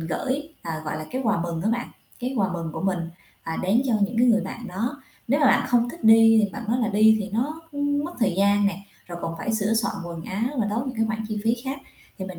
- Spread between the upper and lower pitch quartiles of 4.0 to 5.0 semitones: Yes, average, 4.3 semitones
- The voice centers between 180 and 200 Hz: No, high, 220 Hz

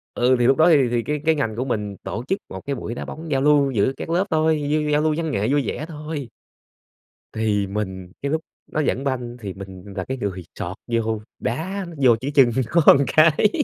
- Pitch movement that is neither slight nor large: No, wide, 5.7 semitones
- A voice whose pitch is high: No, low, 135 Hz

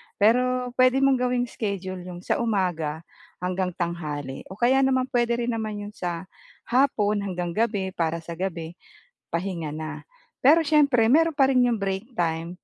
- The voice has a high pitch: Yes, high, 200 Hz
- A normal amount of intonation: No, wide, 6.2 semitones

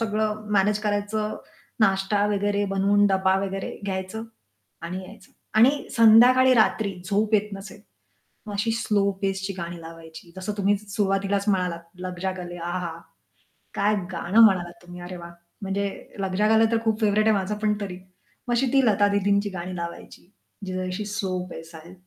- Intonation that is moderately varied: No, narrow, 2.3 semitones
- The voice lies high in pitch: Yes, high, 200 Hz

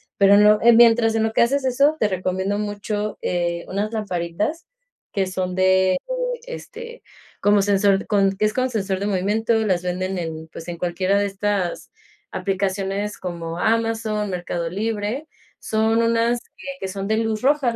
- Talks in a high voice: Yes, high, 205 Hz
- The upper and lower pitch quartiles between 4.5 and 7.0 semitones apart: No, average, 3.0 semitones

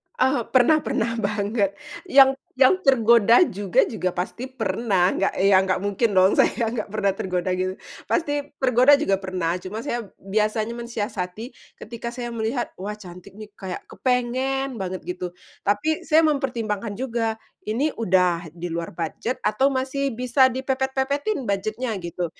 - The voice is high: Yes, high, 225 Hz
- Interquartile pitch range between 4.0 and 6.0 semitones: Yes, average, 5.2 semitones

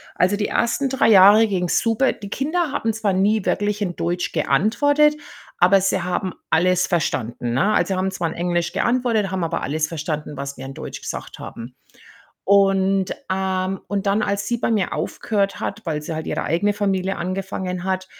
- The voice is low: No, high, 190 Hz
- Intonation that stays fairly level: No, average, 3.1 semitones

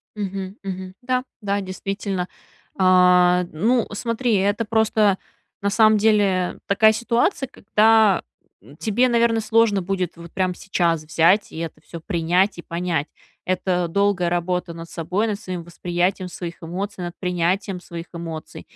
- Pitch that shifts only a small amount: No, average, 3.1 semitones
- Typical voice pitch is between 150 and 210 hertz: Yes, high, 190 Hz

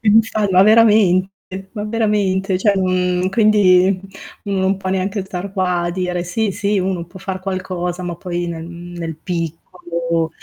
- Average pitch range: No, narrow, 2.2 semitones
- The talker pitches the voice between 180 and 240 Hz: Yes, high, 190 Hz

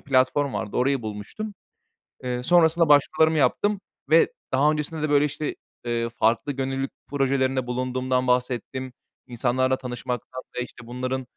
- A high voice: No, low, 130 Hz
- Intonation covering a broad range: No, narrow, 2.6 semitones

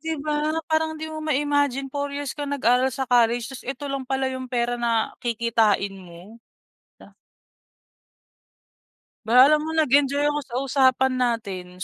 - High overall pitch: Yes, very high, 260 Hz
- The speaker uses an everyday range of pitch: Yes, average, 3.6 semitones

